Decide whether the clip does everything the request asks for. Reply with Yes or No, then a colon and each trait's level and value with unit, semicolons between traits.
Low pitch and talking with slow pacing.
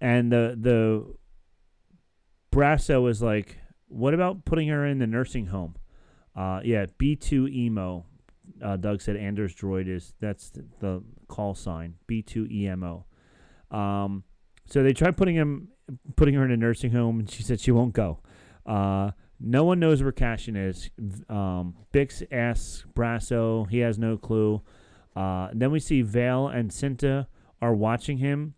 No: low, 115 Hz; average, 150 wpm